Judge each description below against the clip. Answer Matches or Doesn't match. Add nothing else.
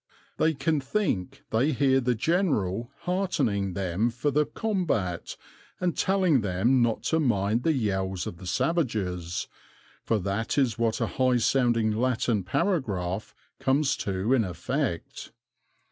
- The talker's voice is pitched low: Matches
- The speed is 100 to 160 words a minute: Matches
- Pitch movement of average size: Doesn't match